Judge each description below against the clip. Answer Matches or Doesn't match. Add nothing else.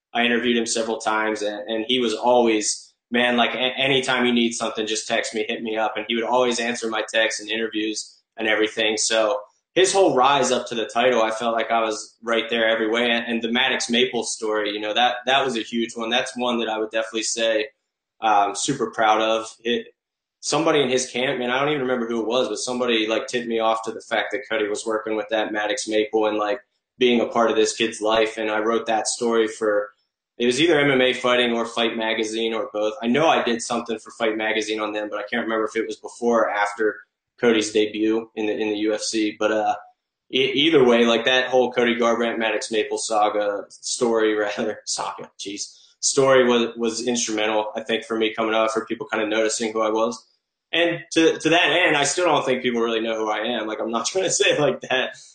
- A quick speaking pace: Matches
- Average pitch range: Doesn't match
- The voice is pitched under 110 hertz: Doesn't match